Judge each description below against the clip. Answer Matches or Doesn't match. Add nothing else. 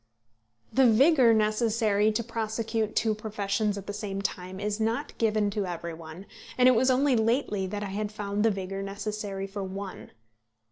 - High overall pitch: Matches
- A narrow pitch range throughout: Matches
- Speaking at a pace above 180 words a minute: Doesn't match